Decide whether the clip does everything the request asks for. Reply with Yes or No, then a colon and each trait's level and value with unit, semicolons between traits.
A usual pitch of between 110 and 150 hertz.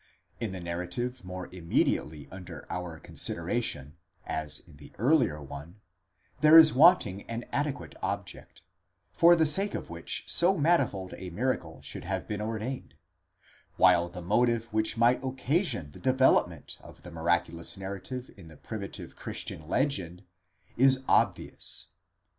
No: low, 100 Hz